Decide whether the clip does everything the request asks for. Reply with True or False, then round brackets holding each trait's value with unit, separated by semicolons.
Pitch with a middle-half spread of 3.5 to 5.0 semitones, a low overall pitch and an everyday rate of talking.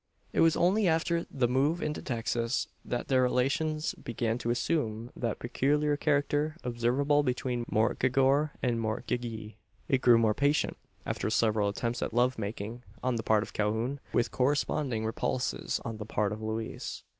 True (4.0 semitones; 125 Hz; 155 wpm)